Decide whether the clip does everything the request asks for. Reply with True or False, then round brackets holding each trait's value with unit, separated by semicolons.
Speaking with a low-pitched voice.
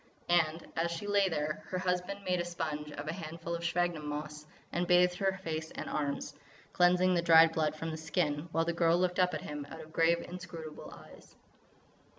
False (170 Hz)